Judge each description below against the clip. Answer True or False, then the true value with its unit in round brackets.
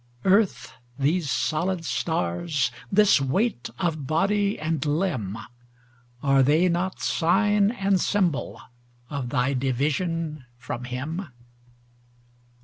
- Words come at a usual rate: False (95 wpm)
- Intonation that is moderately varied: False (6.5 semitones)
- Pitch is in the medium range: True (155 Hz)